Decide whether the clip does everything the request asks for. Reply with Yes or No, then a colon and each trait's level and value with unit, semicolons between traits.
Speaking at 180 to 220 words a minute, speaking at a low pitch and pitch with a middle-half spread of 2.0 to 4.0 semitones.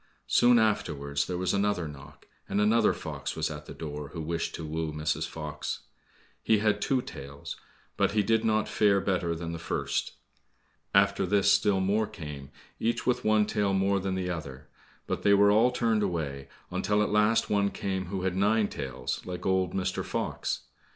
No: average, 185 wpm; very low, 95 Hz; average, 4.4 semitones